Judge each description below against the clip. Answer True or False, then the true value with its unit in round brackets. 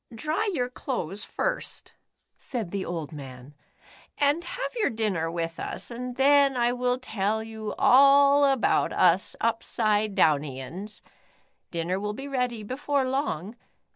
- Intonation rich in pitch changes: True (6.4 semitones)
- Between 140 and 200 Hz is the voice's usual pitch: False (225 Hz)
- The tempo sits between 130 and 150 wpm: True (135 wpm)